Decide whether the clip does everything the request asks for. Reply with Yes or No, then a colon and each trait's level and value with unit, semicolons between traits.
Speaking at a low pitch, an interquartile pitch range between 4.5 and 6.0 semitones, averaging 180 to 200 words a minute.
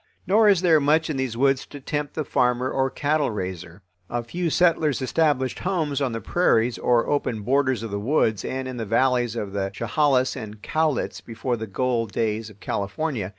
Yes: low, 130 Hz; average, 4.8 semitones; average, 195 wpm